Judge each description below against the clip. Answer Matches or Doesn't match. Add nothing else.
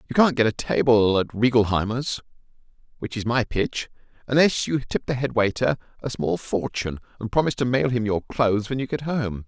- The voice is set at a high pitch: Doesn't match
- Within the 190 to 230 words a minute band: Matches